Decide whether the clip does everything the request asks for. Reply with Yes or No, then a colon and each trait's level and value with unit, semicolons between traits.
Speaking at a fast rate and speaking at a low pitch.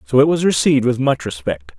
Yes: fast, 235 wpm; low, 125 Hz